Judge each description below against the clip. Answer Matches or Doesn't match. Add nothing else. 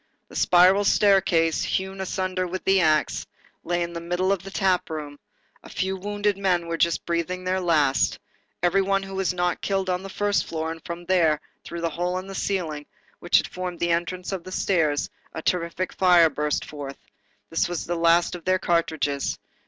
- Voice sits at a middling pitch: Matches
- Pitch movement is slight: Matches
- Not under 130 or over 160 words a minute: Doesn't match